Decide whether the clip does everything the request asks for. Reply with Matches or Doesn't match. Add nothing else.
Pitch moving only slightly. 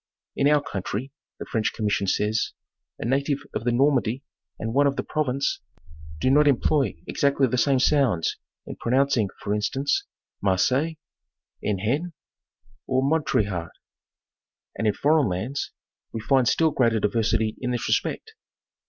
Doesn't match